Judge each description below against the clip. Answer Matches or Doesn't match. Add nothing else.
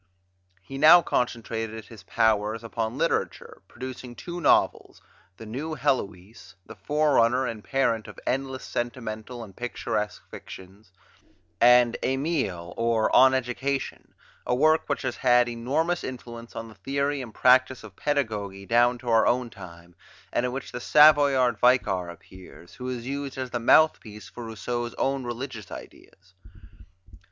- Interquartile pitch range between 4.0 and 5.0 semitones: Doesn't match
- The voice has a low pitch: Matches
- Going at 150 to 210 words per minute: Doesn't match